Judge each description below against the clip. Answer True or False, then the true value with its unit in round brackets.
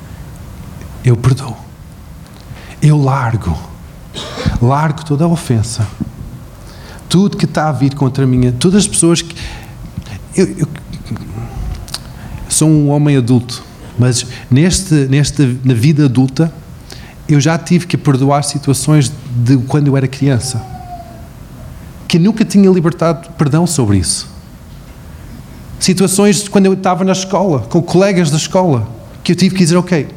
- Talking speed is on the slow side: False (135 wpm)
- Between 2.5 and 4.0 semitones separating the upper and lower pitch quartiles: False (5.4 semitones)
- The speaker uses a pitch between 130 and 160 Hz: True (140 Hz)